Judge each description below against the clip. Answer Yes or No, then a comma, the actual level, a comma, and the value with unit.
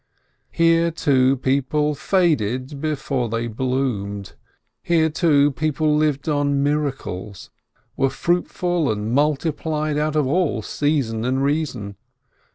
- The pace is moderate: No, slow, 115 wpm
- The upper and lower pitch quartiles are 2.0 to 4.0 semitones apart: Yes, average, 3.3 semitones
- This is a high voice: No, medium, 140 Hz